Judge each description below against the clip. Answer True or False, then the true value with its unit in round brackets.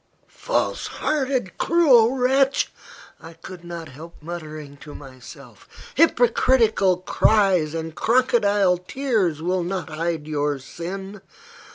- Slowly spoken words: True (105 wpm)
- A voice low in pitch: False (180 Hz)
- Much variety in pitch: True (6.7 semitones)